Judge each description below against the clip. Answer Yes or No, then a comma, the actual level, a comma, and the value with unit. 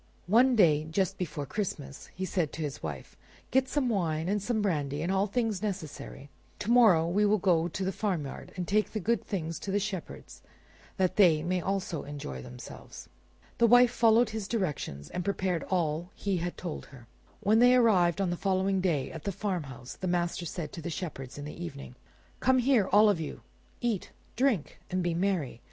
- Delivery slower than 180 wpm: No, average, 195 wpm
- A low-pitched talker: No, medium, 185 Hz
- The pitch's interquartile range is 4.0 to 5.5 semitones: Yes, average, 4.6 semitones